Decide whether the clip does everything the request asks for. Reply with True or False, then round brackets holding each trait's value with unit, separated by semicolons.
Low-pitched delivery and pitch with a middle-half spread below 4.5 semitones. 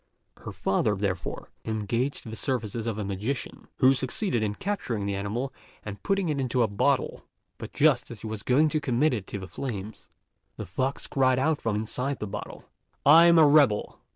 False (120 Hz; 5.0 semitones)